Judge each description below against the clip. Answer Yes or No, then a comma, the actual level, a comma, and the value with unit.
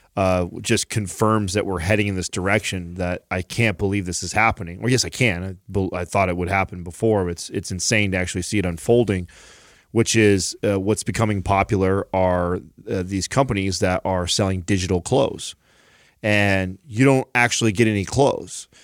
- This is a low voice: Yes, very low, 95 Hz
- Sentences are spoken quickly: No, average, 190 wpm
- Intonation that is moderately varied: Yes, average, 3.1 semitones